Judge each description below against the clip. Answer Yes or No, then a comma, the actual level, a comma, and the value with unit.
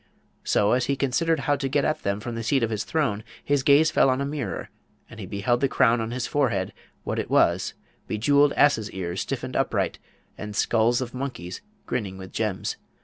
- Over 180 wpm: Yes, average, 200 wpm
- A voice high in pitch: No, low, 120 Hz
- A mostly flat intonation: No, average, 4.8 semitones